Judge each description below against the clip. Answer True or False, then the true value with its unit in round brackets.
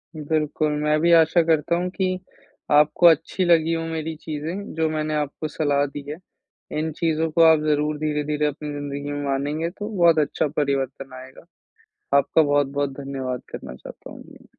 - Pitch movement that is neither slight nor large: False (2.1 semitones)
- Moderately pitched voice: True (150 Hz)